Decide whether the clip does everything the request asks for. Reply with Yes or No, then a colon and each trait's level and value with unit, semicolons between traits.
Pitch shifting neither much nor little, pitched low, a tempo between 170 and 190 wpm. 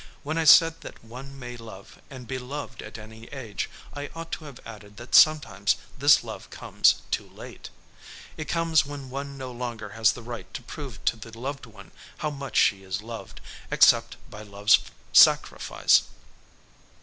Yes: average, 4.4 semitones; low, 125 Hz; average, 175 wpm